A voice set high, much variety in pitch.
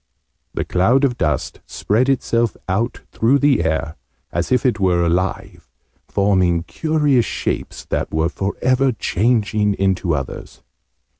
No: low, 105 Hz; wide, 6.0 semitones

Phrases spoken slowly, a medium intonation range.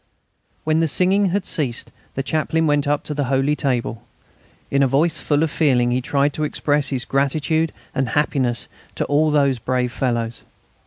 No: average, 175 wpm; average, 3.2 semitones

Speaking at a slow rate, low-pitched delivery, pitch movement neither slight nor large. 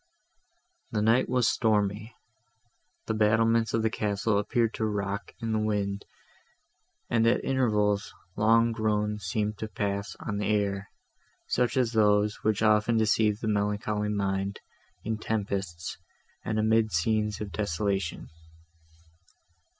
No: slow, 125 wpm; low, 105 Hz; narrow, 1.6 semitones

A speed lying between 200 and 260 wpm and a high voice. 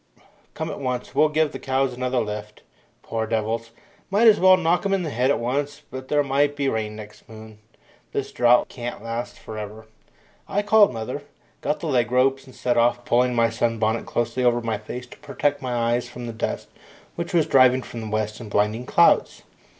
No: fast, 205 wpm; low, 125 Hz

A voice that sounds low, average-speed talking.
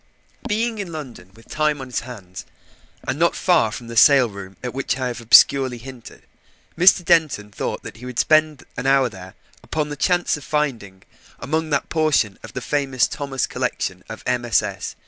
Yes: low, 130 Hz; average, 185 wpm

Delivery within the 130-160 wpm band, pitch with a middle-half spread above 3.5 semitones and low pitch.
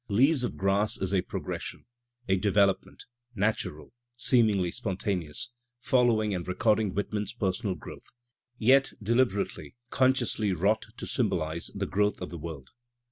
Yes: slow, 135 wpm; average, 3.9 semitones; low, 105 Hz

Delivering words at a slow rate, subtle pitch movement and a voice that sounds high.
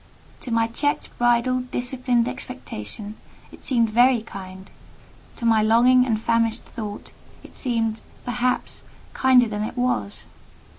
Yes: slow, 130 wpm; narrow, 2.3 semitones; high, 235 Hz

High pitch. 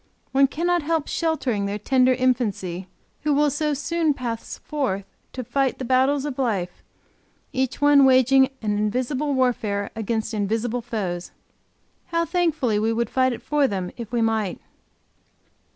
Yes: very high, 255 Hz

